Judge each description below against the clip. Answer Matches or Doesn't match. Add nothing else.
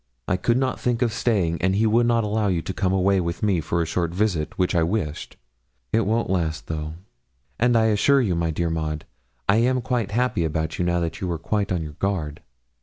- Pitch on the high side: Doesn't match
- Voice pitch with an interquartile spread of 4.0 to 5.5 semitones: Matches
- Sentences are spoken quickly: Matches